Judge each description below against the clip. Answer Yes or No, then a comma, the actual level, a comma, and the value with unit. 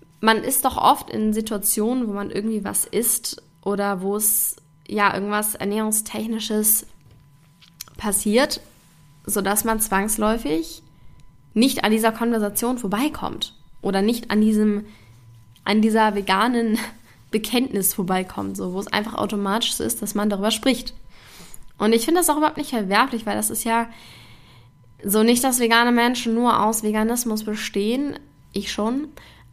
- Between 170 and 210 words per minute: No, average, 140 wpm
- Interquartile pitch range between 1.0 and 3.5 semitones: Yes, average, 3.2 semitones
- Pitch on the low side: No, high, 215 Hz